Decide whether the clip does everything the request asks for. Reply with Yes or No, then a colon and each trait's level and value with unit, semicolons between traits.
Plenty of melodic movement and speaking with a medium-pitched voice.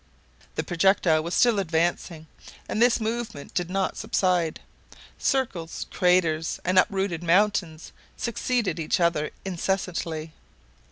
No: average, 3.6 semitones; medium, 180 Hz